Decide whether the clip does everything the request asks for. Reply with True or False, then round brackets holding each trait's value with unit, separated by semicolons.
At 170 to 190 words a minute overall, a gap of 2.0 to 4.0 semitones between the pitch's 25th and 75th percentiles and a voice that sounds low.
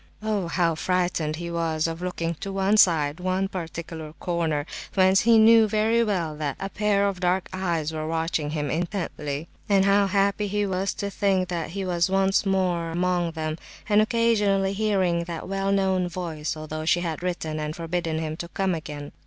False (180 wpm; 3.2 semitones; 180 Hz)